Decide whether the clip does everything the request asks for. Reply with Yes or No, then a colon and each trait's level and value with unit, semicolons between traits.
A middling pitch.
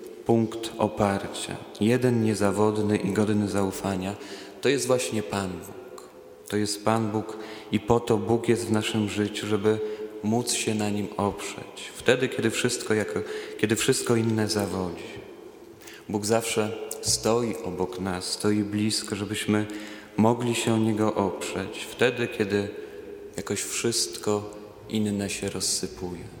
No: low, 105 Hz